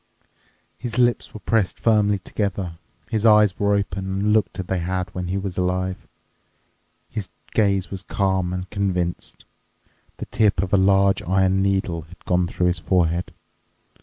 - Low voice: Yes, very low, 95 Hz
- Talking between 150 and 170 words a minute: Yes, average, 160 wpm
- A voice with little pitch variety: Yes, narrow, 1.9 semitones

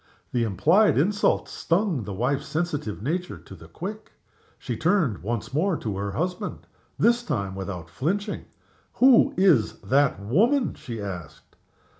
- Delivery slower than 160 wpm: Yes, average, 140 wpm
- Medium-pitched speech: Yes, medium, 145 Hz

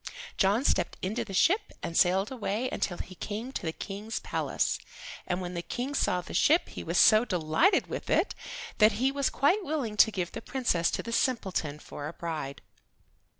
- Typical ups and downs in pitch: No, wide, 6.4 semitones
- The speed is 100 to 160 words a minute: No, average, 195 wpm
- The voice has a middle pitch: No, high, 210 Hz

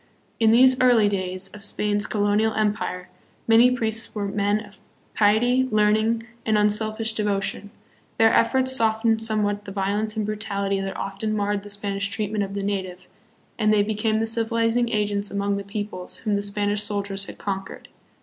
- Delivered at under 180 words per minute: Yes, average, 170 wpm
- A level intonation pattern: Yes, narrow, 1.7 semitones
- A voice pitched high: Yes, high, 210 Hz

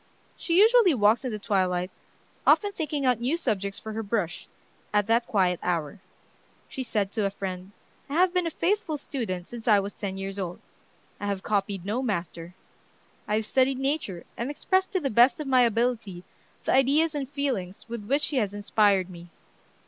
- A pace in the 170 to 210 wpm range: Yes, average, 185 wpm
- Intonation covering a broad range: Yes, wide, 5.9 semitones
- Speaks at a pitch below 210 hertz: No, high, 220 Hz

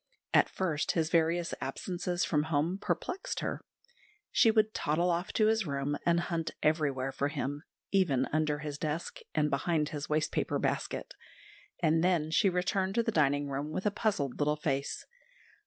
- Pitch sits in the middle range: Yes, medium, 160 Hz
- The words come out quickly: No, average, 170 wpm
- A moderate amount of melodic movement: Yes, average, 3.6 semitones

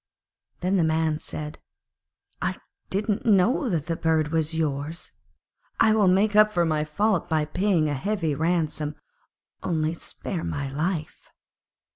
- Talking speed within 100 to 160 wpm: Yes, average, 140 wpm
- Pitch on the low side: No, medium, 165 Hz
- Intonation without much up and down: No, average, 4.0 semitones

